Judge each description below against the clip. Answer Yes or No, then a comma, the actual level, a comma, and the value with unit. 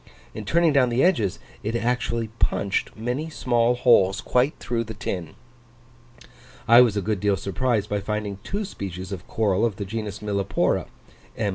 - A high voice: No, low, 110 Hz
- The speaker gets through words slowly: No, average, 165 wpm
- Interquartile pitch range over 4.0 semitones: No, average, 3.5 semitones